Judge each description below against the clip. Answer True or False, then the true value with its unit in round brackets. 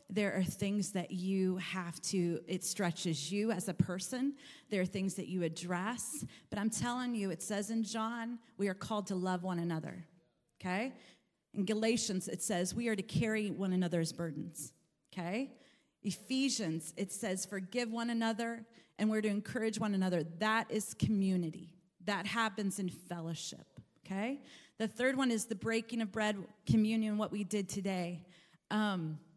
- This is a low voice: False (200 Hz)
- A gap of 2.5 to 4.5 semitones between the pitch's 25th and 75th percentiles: True (3.7 semitones)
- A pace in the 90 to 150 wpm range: False (165 wpm)